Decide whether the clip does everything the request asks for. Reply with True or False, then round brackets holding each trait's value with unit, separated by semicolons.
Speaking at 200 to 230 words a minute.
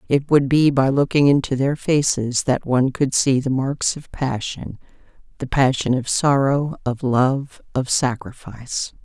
False (155 wpm)